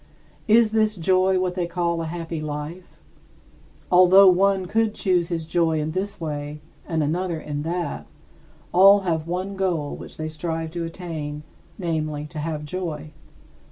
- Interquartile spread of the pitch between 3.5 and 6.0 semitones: No, average, 2.9 semitones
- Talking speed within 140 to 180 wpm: Yes, average, 155 wpm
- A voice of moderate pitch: Yes, medium, 170 Hz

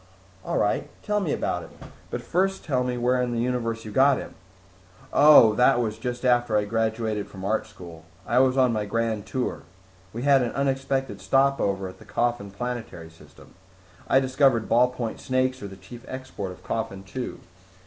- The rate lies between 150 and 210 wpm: Yes, average, 180 wpm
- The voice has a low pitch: Yes, low, 120 Hz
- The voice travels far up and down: No, average, 3.4 semitones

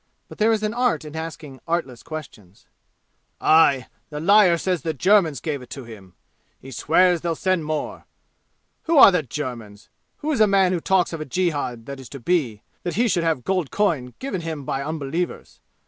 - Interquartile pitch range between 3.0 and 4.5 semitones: No, wide, 5.4 semitones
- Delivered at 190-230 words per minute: Yes, average, 195 wpm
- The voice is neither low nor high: Yes, medium, 160 Hz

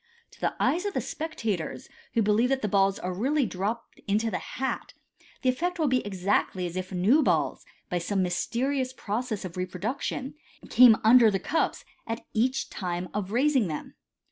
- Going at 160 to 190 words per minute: Yes, average, 180 wpm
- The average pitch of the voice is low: No, high, 220 Hz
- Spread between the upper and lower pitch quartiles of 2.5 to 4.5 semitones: No, wide, 5.6 semitones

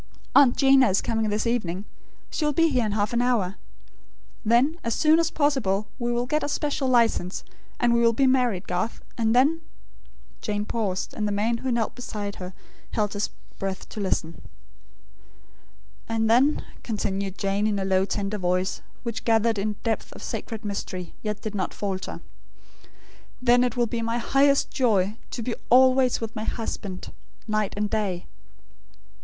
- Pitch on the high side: Yes, high, 225 Hz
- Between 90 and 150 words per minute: No, average, 170 wpm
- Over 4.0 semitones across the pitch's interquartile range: No, average, 3.5 semitones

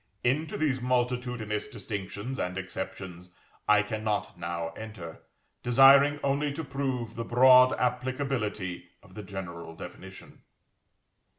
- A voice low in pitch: Yes, low, 115 Hz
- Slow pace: Yes, slow, 110 wpm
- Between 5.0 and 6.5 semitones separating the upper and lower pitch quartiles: Yes, wide, 5.5 semitones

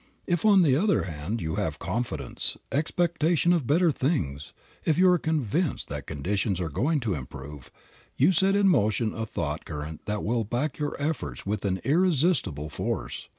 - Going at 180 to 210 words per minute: No, average, 170 wpm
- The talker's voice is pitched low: Yes, low, 120 Hz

